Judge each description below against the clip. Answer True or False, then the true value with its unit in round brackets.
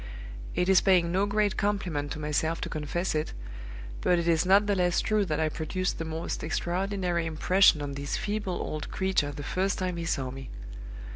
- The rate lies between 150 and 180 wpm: False (195 wpm)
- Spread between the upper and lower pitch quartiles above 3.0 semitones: True (3.7 semitones)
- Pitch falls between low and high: True (175 Hz)